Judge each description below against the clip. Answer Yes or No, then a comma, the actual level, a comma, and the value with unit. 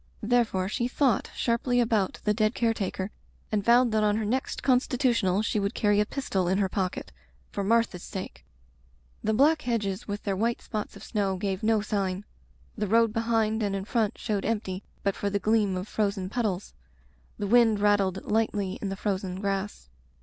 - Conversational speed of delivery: Yes, average, 185 wpm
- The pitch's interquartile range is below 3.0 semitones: Yes, narrow, 2.6 semitones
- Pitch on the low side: No, high, 210 Hz